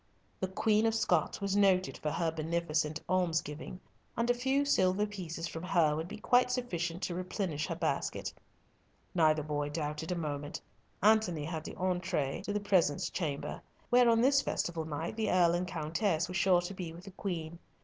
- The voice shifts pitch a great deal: No, average, 4.0 semitones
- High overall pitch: No, medium, 175 Hz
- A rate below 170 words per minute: No, average, 180 wpm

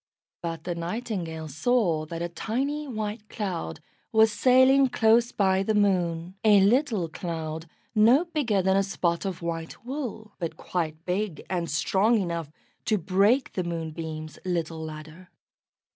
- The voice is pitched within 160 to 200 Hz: Yes, high, 190 Hz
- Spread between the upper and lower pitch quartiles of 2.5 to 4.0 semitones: No, average, 4.9 semitones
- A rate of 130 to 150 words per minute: Yes, average, 145 wpm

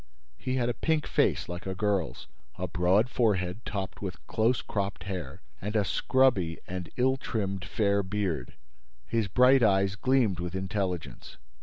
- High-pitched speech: No, low, 100 Hz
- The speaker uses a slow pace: No, average, 155 wpm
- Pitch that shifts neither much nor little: Yes, average, 4.0 semitones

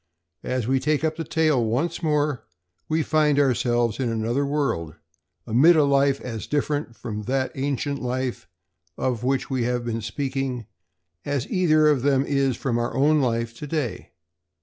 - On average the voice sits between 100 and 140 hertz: Yes, low, 135 Hz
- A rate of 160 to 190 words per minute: Yes, average, 165 wpm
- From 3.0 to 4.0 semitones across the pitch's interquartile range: Yes, average, 3.7 semitones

